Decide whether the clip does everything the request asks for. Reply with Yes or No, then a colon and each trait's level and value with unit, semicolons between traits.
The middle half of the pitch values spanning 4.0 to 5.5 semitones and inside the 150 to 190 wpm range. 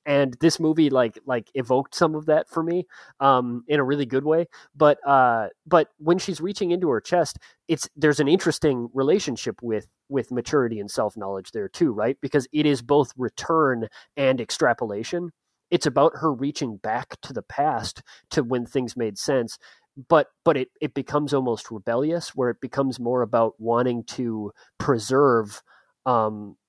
Yes: average, 4.3 semitones; average, 170 wpm